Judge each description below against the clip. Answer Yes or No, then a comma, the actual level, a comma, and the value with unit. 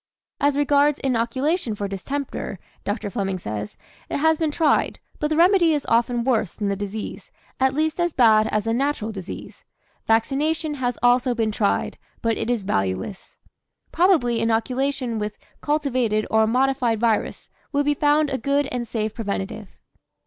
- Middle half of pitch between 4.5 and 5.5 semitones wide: Yes, average, 5.1 semitones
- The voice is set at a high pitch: Yes, high, 245 Hz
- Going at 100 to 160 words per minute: Yes, average, 155 wpm